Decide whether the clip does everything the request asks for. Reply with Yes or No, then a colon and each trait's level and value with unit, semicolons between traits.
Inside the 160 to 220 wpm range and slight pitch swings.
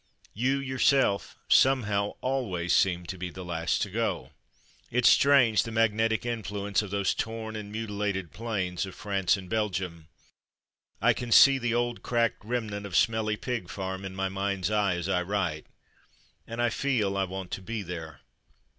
No: average, 170 wpm; average, 3.5 semitones